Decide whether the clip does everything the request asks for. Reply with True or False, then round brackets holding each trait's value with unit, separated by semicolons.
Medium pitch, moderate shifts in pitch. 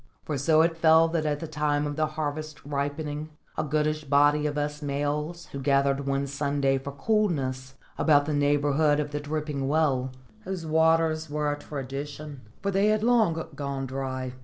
False (150 Hz; 1.9 semitones)